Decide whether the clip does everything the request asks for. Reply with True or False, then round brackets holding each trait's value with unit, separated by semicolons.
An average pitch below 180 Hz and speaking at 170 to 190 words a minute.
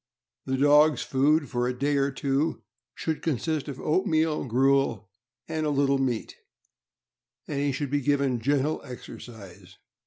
False (140 Hz; 145 wpm)